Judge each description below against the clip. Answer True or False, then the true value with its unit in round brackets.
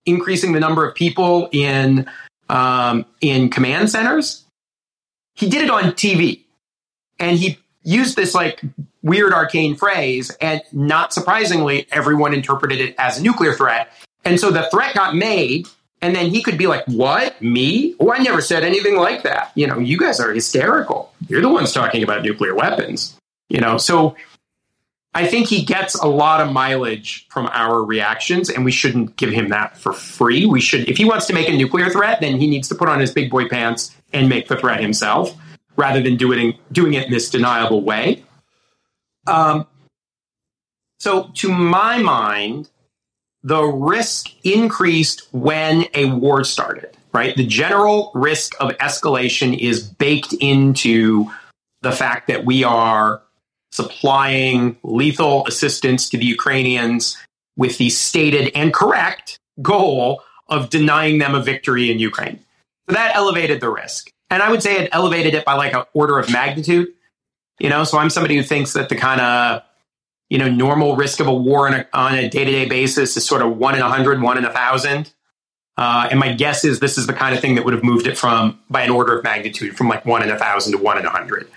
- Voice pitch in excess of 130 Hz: True (140 Hz)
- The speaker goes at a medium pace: True (190 wpm)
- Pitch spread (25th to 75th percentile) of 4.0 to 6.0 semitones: True (4.5 semitones)